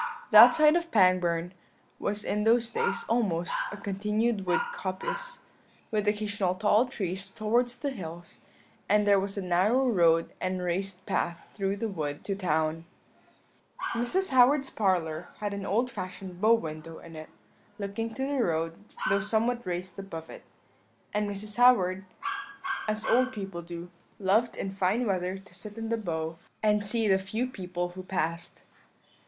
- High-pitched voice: Yes, high, 200 Hz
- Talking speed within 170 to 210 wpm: No, average, 160 wpm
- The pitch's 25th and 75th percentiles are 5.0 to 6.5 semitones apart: No, average, 4.0 semitones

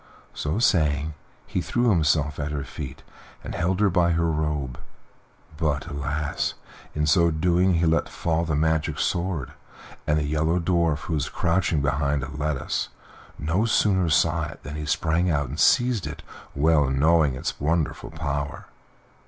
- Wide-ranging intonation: No, narrow, 2.5 semitones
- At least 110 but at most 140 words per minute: No, average, 160 wpm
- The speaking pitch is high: No, very low, 80 Hz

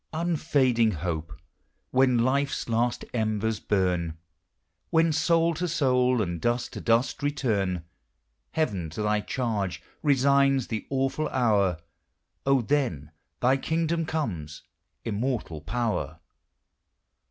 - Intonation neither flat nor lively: No, wide, 5.9 semitones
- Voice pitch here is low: Yes, low, 120 Hz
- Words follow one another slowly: Yes, slow, 115 wpm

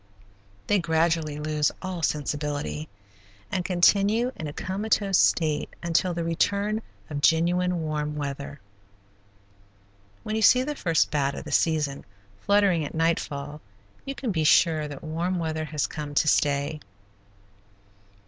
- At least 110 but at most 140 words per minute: Yes, slow, 135 wpm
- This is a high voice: No, medium, 160 Hz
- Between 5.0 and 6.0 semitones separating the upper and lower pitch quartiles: No, average, 3.7 semitones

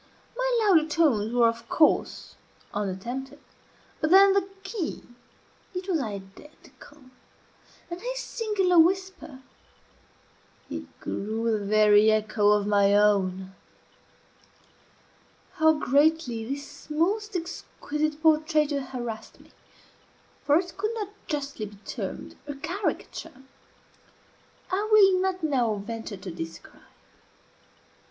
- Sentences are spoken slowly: Yes, slow, 105 wpm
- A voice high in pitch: Yes, very high, 295 Hz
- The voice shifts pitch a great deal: Yes, wide, 8.7 semitones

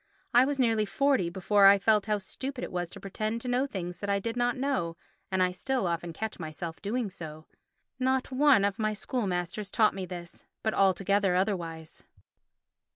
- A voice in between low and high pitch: No, high, 200 Hz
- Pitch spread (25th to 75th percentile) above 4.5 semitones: Yes, average, 5.3 semitones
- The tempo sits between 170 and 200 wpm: Yes, average, 190 wpm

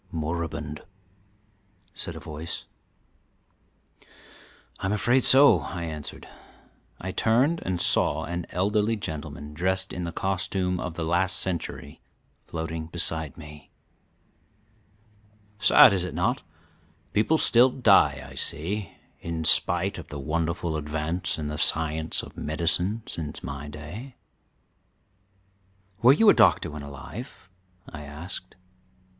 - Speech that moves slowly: Yes, slow, 120 wpm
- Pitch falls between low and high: No, very low, 85 Hz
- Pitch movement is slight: No, average, 3.9 semitones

